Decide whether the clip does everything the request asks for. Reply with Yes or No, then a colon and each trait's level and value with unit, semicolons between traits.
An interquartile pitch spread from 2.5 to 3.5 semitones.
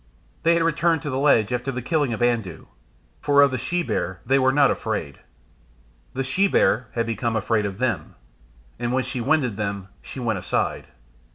No: average, 4.1 semitones